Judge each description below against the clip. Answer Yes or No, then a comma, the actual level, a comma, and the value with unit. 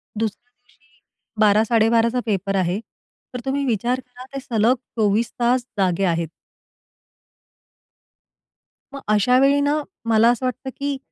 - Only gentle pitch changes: No, average, 3.2 semitones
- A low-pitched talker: No, high, 235 Hz